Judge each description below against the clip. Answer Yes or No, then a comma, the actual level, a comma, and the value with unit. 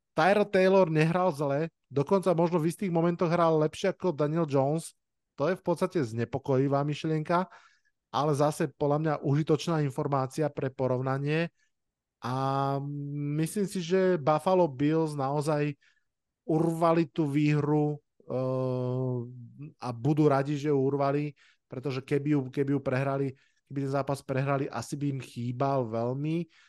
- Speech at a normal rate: Yes, average, 135 wpm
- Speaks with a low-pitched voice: No, medium, 150 Hz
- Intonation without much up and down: No, average, 3.2 semitones